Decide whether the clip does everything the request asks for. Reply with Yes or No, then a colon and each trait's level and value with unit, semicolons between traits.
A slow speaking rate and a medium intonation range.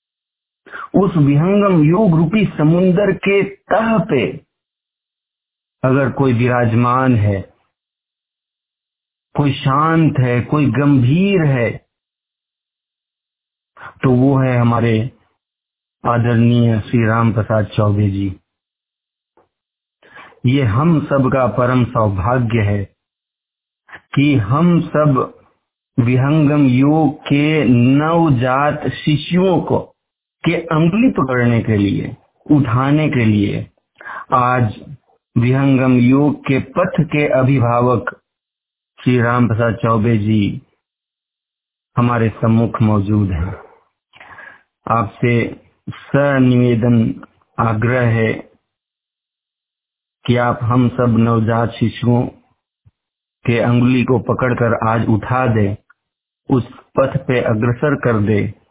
Yes: slow, 95 wpm; average, 3.8 semitones